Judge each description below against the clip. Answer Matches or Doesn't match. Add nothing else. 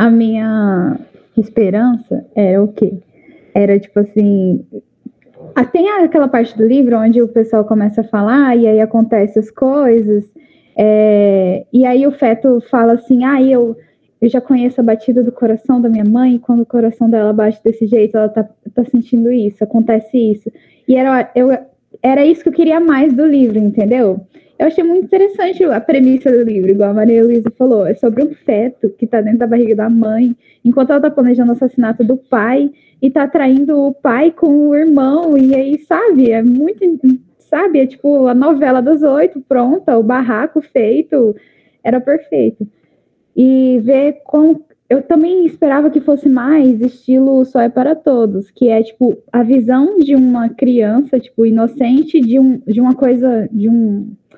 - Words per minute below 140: Doesn't match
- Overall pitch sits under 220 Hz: Doesn't match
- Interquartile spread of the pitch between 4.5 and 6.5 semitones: Doesn't match